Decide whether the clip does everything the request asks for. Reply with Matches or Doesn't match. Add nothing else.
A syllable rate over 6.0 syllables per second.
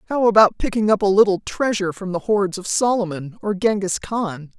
Doesn't match